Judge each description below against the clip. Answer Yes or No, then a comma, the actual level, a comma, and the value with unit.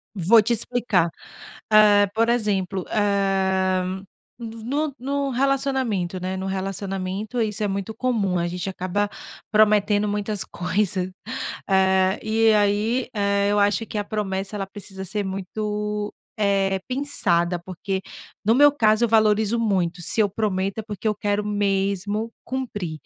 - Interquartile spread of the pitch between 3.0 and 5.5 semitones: No, narrow, 2.4 semitones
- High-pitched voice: Yes, high, 205 Hz